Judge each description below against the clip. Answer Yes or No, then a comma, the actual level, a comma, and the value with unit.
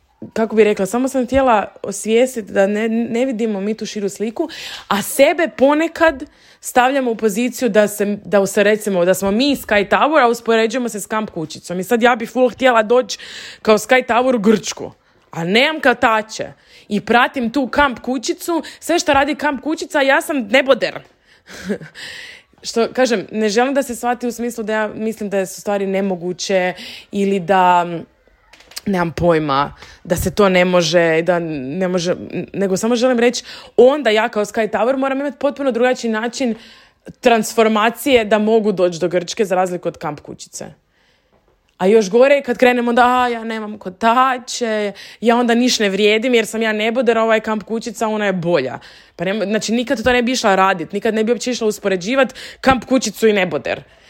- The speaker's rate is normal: No, fast, 175 wpm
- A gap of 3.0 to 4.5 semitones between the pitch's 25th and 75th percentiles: Yes, average, 3.9 semitones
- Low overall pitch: No, high, 225 Hz